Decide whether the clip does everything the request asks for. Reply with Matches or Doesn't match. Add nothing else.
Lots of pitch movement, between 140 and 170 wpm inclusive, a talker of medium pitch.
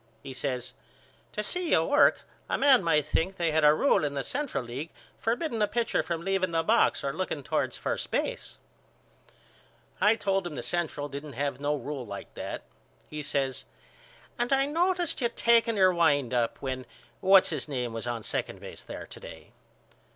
Doesn't match